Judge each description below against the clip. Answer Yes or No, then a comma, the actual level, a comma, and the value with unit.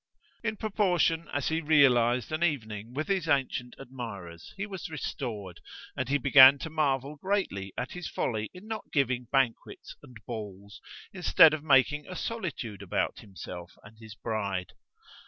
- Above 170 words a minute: No, average, 155 wpm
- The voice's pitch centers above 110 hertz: Yes, low, 135 Hz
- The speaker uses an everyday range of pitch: No, wide, 6.5 semitones